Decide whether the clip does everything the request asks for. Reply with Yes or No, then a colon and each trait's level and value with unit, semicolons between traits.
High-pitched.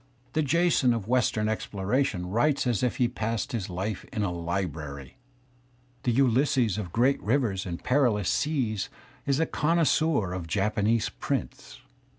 No: low, 115 Hz